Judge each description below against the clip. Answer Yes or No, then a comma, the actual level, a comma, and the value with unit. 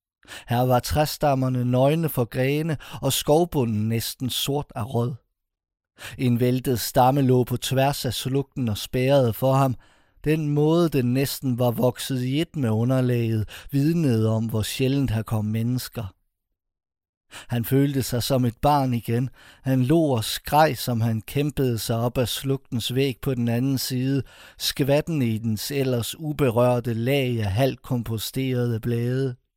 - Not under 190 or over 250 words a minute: No, average, 150 wpm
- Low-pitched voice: Yes, low, 125 Hz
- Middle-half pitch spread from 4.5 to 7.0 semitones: No, average, 2.8 semitones